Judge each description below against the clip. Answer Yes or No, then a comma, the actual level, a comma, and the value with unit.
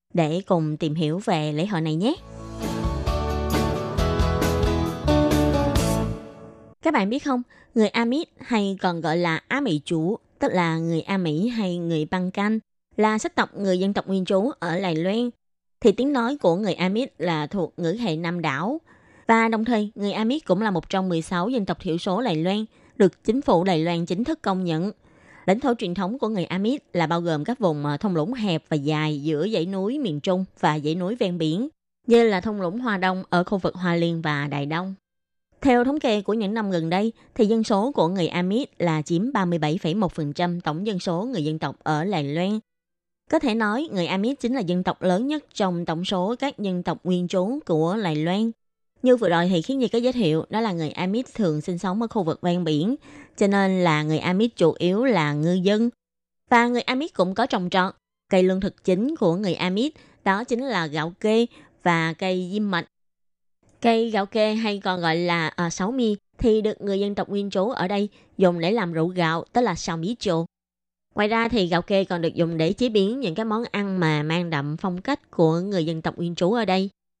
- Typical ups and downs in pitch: Yes, average, 5.0 semitones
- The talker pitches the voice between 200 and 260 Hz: No, medium, 185 Hz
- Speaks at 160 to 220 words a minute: Yes, average, 215 wpm